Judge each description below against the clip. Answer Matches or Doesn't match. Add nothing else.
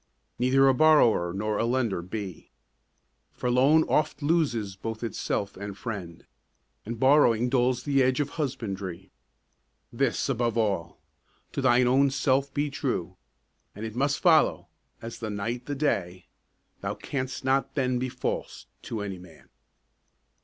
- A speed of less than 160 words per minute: Matches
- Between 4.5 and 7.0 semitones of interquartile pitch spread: Matches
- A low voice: Matches